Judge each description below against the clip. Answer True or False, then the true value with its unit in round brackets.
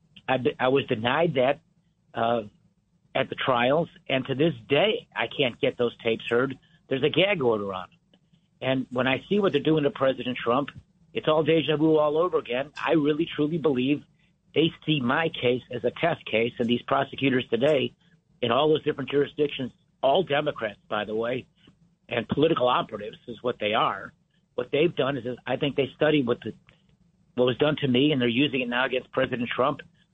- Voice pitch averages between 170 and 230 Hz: False (135 Hz)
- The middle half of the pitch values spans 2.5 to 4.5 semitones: True (4.1 semitones)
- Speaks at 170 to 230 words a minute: True (195 wpm)